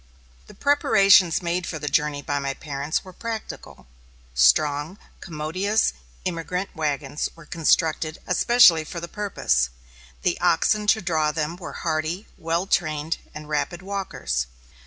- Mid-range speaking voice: Yes, medium, 165 Hz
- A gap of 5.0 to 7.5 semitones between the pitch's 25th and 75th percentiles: No, average, 3.6 semitones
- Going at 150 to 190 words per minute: No, slow, 135 wpm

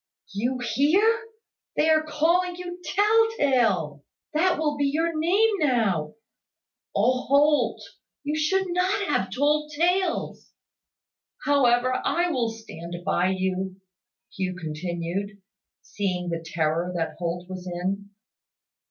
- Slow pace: Yes, slow, 115 wpm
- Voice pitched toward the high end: Yes, very high, 255 Hz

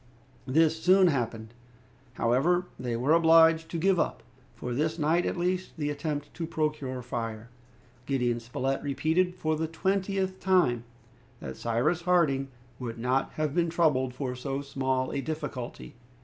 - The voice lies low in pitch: No, medium, 150 Hz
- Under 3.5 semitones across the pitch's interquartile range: No, average, 4.8 semitones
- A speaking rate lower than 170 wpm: Yes, average, 150 wpm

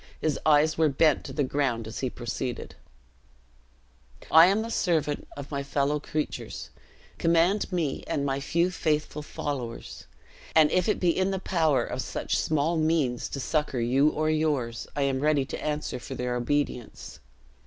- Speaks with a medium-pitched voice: Yes, medium, 150 Hz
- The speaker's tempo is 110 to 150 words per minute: No, average, 165 wpm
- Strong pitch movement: No, average, 2.9 semitones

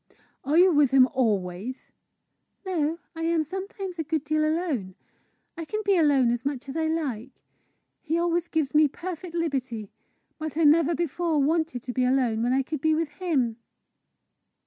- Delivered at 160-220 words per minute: Yes, average, 170 wpm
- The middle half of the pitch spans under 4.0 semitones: No, average, 4.3 semitones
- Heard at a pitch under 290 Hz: No, very high, 310 Hz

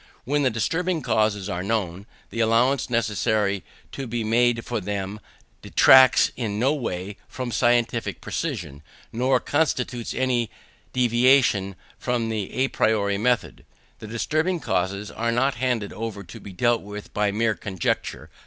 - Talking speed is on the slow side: No, average, 145 wpm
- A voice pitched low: Yes, low, 115 Hz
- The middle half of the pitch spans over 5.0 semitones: No, average, 3.5 semitones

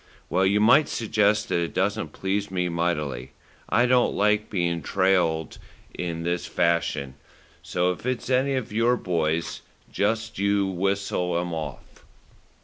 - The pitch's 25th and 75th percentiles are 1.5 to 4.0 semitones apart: Yes, average, 3.7 semitones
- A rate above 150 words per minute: No, average, 140 wpm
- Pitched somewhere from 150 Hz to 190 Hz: No, very low, 95 Hz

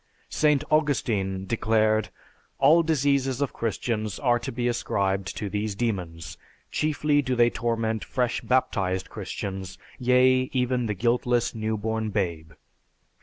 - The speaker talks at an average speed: No, slow, 125 wpm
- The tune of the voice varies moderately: Yes, average, 4.0 semitones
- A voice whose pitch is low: Yes, low, 115 Hz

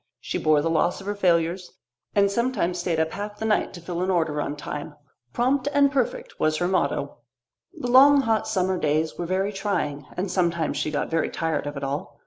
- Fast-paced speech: Yes, fast, 215 wpm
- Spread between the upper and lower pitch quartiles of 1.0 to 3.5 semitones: No, average, 4.5 semitones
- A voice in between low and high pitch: Yes, medium, 180 Hz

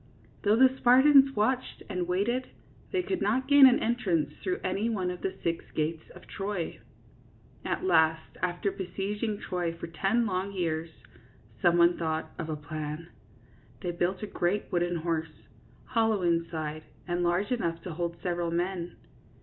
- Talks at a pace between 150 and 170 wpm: Yes, average, 160 wpm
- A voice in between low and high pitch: Yes, medium, 180 Hz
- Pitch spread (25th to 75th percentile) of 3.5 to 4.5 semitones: Yes, average, 4.0 semitones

